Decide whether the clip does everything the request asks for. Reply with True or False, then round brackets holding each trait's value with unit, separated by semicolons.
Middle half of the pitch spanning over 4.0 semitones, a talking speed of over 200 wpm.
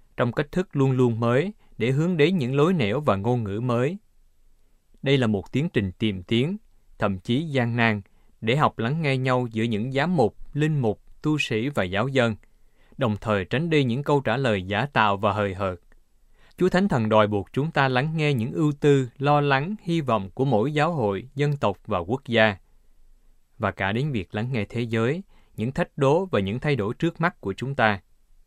True (5.4 semitones; 215 wpm)